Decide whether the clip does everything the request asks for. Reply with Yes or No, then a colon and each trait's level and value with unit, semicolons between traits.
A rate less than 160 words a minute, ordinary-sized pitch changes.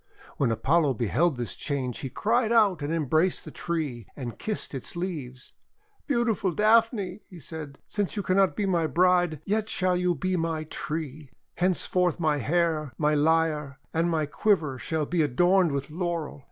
No: average, 165 wpm; average, 4.0 semitones